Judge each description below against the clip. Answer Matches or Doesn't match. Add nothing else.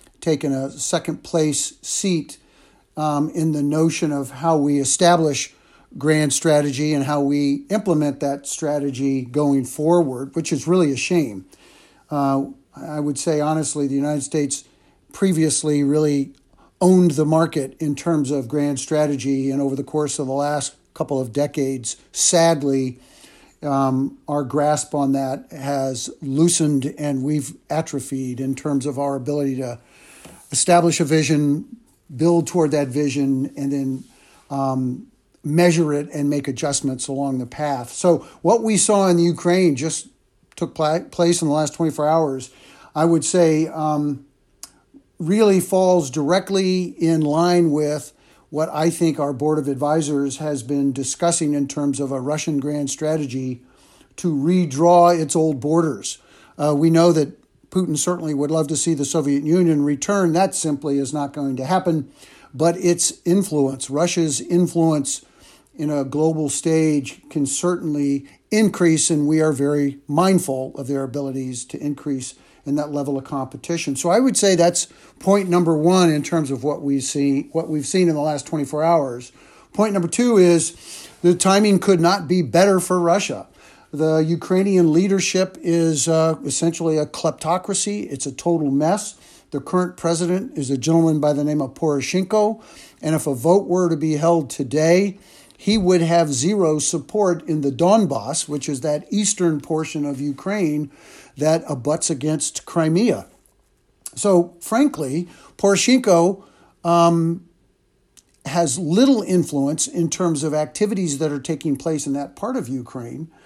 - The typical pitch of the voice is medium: Matches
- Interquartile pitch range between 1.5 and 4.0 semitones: Matches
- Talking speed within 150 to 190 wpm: Matches